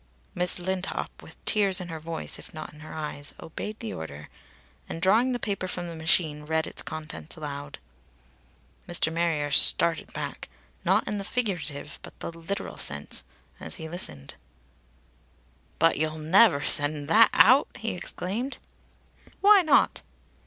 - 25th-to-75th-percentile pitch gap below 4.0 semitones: No, average, 4.4 semitones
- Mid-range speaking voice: Yes, medium, 165 Hz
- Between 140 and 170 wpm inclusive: Yes, average, 150 wpm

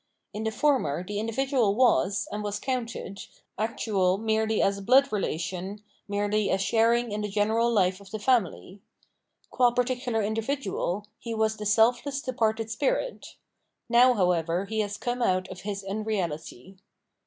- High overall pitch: Yes, high, 215 Hz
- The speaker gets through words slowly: No, average, 150 wpm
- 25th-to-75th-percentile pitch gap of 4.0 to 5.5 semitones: No, average, 3.2 semitones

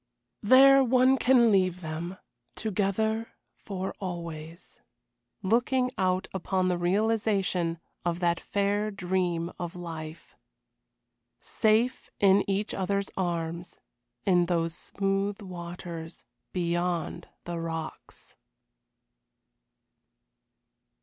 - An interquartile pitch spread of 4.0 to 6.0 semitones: No, average, 3.2 semitones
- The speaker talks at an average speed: No, slow, 90 wpm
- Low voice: No, medium, 185 Hz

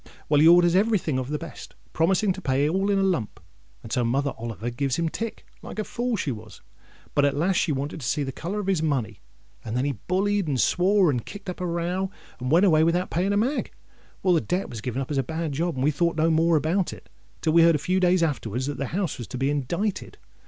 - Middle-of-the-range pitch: Yes, medium, 160 Hz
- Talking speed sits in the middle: No, fast, 260 wpm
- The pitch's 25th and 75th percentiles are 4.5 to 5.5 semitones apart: Yes, average, 5.2 semitones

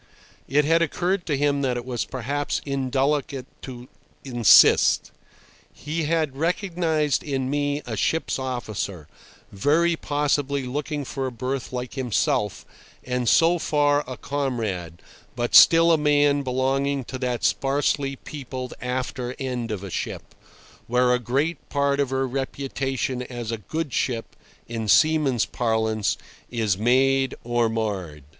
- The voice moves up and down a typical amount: Yes, average, 3.1 semitones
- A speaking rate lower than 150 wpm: Yes, slow, 135 wpm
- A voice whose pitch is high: No, low, 135 Hz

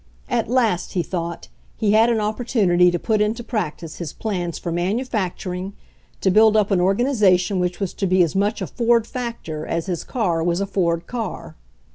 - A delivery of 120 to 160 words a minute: No, average, 185 wpm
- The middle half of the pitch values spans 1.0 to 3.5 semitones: No, average, 3.9 semitones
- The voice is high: Yes, high, 195 Hz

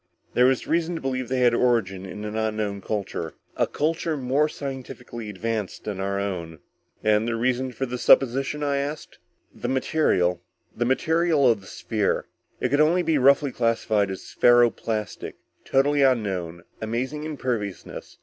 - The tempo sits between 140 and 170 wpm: Yes, average, 160 wpm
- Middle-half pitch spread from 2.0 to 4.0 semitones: No, average, 4.7 semitones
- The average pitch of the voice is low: Yes, low, 120 Hz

